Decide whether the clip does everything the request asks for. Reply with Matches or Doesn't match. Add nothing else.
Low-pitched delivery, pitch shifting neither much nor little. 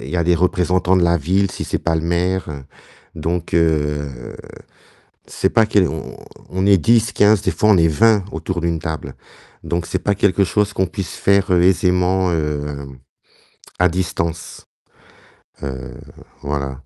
Matches